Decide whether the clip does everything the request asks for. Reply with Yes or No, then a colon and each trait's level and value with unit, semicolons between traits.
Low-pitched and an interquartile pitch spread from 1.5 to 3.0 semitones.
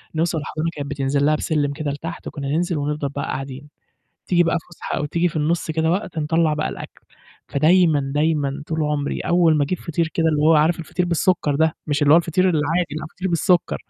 No: medium, 155 Hz; narrow, 2.4 semitones